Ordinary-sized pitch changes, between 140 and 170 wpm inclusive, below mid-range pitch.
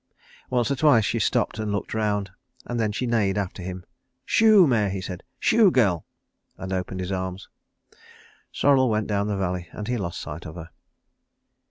No: average, 4.2 semitones; average, 180 wpm; low, 100 Hz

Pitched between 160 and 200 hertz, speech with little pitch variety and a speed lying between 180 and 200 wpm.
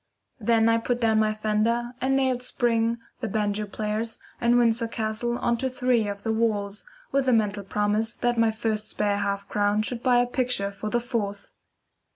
No: high, 225 Hz; narrow, 2.3 semitones; average, 190 wpm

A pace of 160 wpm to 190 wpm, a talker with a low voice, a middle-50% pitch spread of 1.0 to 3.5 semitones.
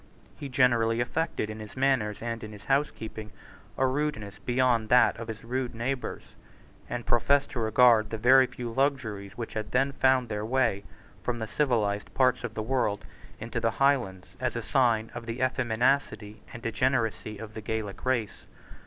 Yes: average, 170 wpm; low, 115 Hz; average, 3.1 semitones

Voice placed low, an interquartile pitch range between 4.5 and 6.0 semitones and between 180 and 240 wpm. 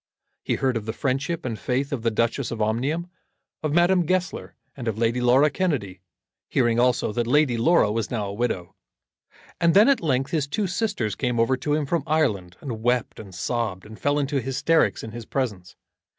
Yes: low, 125 Hz; average, 4.8 semitones; average, 195 wpm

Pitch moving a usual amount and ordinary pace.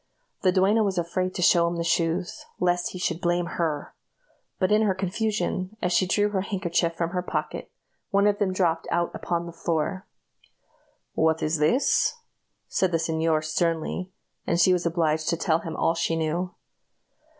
No: narrow, 2.2 semitones; average, 175 wpm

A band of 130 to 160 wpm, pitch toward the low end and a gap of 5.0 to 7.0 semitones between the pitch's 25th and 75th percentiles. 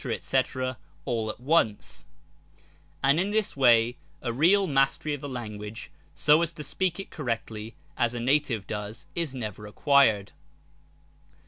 Yes: average, 140 wpm; low, 130 Hz; average, 5.3 semitones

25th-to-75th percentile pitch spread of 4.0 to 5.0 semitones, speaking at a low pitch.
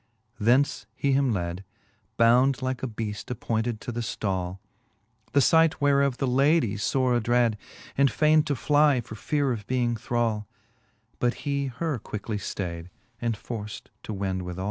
Yes: average, 4.6 semitones; low, 120 Hz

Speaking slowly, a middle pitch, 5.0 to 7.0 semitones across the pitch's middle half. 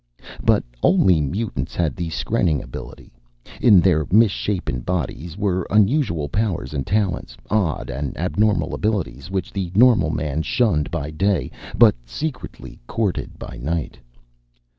No: slow, 130 wpm; very low, 90 Hz; wide, 5.4 semitones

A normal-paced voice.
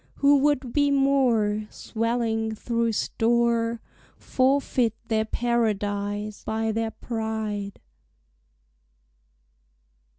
No: slow, 75 wpm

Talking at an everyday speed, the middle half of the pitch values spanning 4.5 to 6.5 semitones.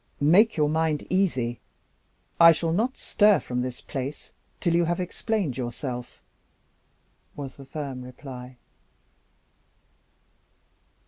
No: slow, 110 wpm; average, 5.2 semitones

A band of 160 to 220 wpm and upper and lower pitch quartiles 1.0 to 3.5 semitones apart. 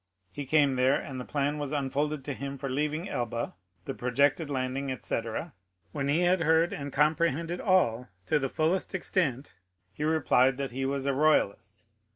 Yes: average, 175 wpm; average, 2.9 semitones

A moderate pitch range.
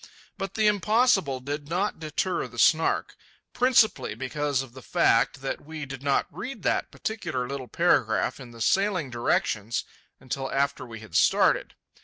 No: wide, 6.8 semitones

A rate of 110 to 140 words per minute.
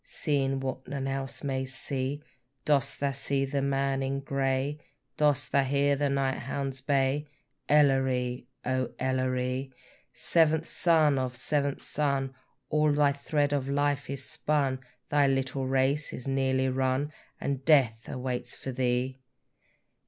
Yes: slow, 135 wpm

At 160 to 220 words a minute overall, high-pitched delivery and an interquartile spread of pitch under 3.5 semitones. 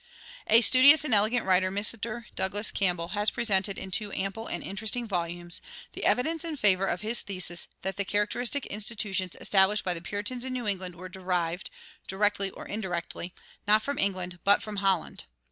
Yes: average, 175 wpm; high, 200 Hz; average, 3.1 semitones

